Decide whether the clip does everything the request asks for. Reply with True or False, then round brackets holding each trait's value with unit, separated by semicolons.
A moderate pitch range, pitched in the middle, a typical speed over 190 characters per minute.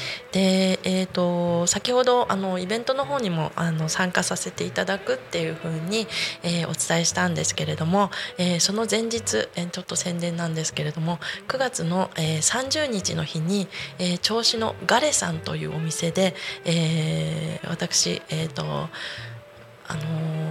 True (3.9 semitones; 175 Hz; 295 characters per minute)